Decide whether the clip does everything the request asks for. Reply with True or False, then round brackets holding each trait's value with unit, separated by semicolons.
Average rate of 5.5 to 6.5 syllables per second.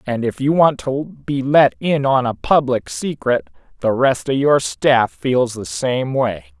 False (3.8 syllables/s)